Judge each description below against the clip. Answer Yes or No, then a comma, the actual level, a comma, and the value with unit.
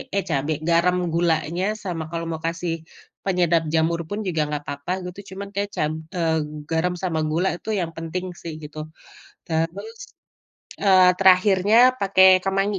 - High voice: No, medium, 175 Hz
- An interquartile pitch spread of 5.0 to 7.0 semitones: No, average, 2.7 semitones